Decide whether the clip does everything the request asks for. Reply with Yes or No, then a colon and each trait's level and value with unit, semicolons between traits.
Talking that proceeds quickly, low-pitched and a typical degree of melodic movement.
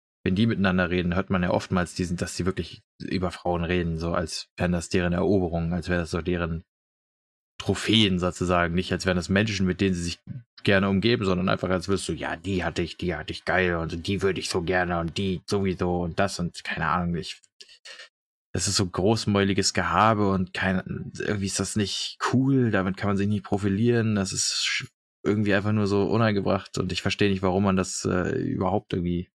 No: fast, 210 wpm; very low, 95 Hz; narrow, 2.1 semitones